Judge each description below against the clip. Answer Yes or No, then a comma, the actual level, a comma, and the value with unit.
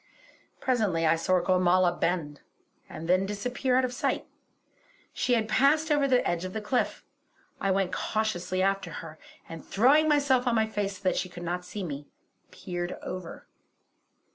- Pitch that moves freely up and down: Yes, wide, 5.8 semitones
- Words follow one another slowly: No, average, 165 wpm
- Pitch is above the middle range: Yes, high, 195 Hz